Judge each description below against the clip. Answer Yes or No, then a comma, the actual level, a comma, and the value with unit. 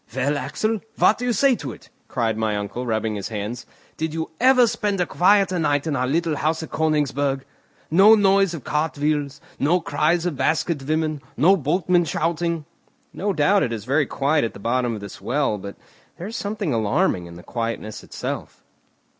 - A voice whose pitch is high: No, medium, 150 Hz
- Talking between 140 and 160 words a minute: No, average, 190 wpm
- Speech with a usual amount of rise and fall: No, wide, 5.9 semitones